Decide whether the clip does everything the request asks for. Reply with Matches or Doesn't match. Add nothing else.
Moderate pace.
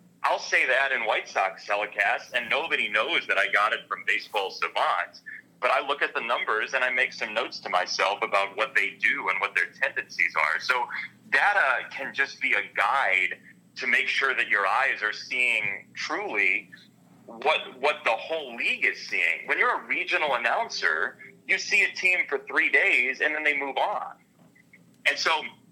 Matches